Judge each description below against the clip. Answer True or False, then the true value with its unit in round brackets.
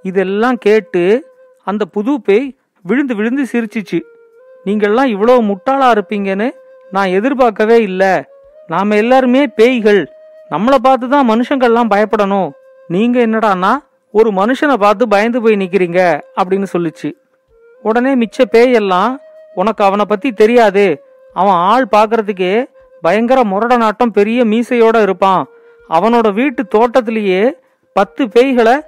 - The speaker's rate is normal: True (110 wpm)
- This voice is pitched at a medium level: False (230 Hz)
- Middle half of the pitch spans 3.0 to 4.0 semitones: False (4.6 semitones)